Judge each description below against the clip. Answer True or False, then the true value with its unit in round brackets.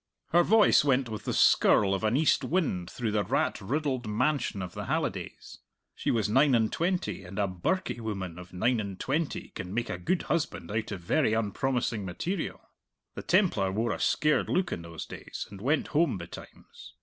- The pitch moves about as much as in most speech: False (7.6 semitones)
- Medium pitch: False (115 Hz)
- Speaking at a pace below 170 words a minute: False (190 wpm)